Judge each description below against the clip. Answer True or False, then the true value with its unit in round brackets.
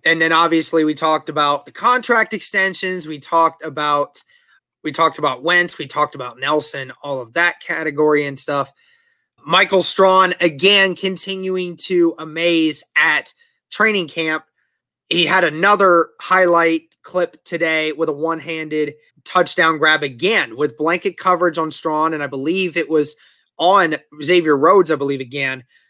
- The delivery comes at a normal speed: True (150 wpm)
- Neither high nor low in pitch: True (165 Hz)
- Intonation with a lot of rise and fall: False (3.3 semitones)